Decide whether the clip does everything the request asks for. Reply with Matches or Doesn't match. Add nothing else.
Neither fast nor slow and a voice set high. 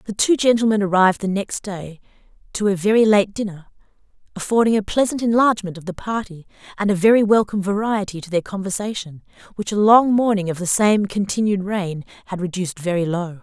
Matches